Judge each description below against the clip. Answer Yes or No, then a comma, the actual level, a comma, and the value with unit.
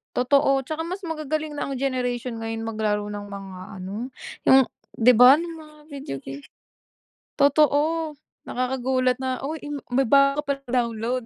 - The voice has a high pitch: Yes, very high, 265 Hz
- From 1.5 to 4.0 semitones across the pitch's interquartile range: No, average, 4.4 semitones